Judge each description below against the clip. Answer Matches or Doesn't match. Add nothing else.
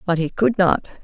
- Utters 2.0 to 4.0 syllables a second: Doesn't match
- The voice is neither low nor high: Matches